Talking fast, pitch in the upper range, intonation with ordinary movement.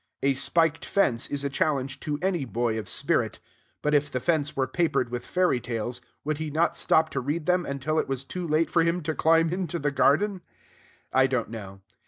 No: fast, 210 wpm; medium, 145 Hz; average, 4.0 semitones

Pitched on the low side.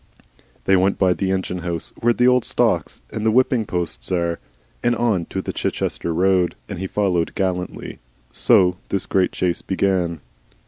Yes: very low, 95 Hz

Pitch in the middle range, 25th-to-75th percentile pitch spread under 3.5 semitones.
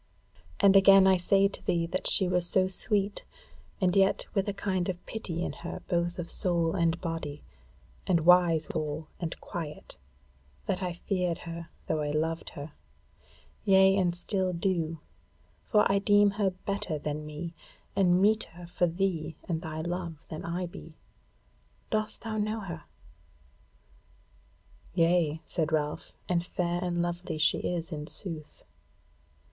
Yes: medium, 175 Hz; average, 2.7 semitones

